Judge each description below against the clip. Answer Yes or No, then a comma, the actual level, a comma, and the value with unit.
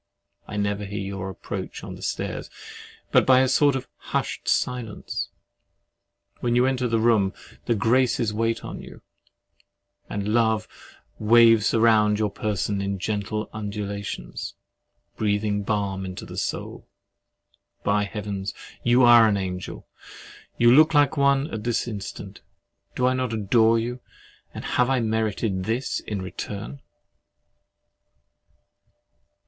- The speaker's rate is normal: No, slow, 125 wpm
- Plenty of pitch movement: No, average, 2.8 semitones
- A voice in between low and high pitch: No, low, 110 Hz